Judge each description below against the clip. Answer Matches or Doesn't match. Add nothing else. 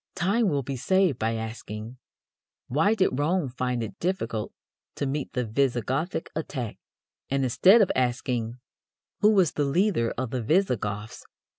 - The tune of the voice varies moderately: Doesn't match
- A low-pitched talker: Matches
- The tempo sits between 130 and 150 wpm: Matches